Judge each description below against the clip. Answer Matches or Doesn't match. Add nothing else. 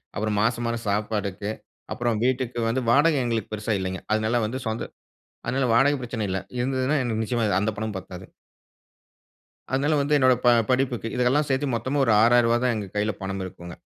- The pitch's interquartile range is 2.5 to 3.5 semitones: Matches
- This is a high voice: Doesn't match